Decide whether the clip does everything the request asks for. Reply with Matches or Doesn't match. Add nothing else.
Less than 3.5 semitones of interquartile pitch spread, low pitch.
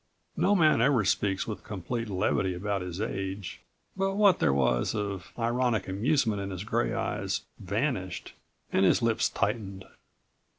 Doesn't match